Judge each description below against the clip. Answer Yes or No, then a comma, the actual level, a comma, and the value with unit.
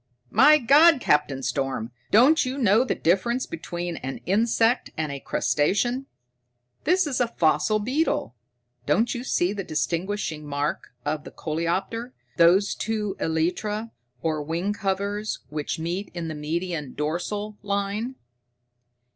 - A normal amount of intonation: No, wide, 6.3 semitones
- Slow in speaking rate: Yes, slow, 130 wpm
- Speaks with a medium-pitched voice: No, high, 195 Hz